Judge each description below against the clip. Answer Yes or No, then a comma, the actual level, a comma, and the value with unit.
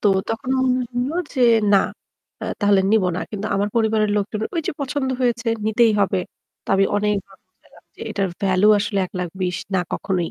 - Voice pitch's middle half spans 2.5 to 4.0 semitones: Yes, average, 2.8 semitones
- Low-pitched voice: No, high, 205 Hz